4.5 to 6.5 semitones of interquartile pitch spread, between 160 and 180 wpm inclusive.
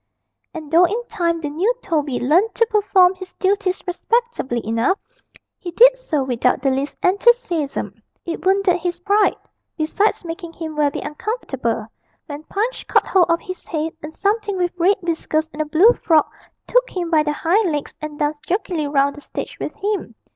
Yes: average, 4.9 semitones; average, 175 wpm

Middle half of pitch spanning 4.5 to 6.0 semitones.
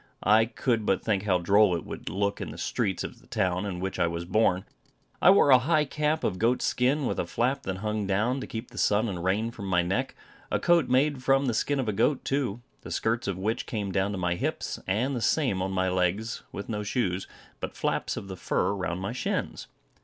Yes: average, 4.9 semitones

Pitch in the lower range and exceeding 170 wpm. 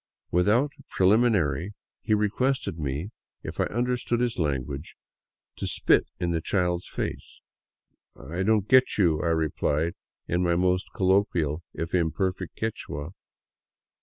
No: very low, 90 Hz; slow, 135 wpm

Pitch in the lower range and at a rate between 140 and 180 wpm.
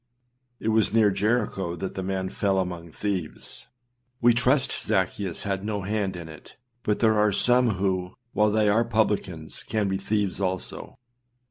Yes: low, 100 Hz; average, 160 wpm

